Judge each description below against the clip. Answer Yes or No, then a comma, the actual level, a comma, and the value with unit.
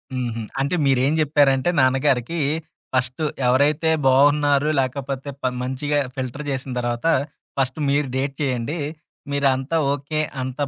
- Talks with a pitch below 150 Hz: Yes, low, 135 Hz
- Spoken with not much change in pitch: Yes, narrow, 2.0 semitones